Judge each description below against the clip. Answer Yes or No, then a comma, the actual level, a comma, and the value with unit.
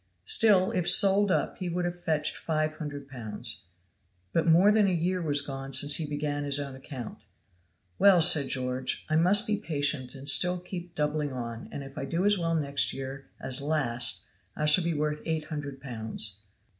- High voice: No, medium, 150 Hz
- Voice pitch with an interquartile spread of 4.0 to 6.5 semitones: Yes, average, 4.3 semitones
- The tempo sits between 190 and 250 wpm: Yes, average, 195 wpm